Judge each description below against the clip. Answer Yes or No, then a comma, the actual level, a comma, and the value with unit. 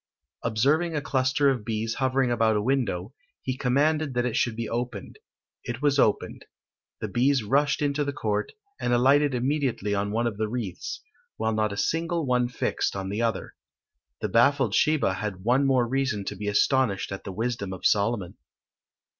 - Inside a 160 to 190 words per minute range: Yes, average, 180 wpm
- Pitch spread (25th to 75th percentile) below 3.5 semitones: No, average, 4.3 semitones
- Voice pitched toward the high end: No, low, 120 Hz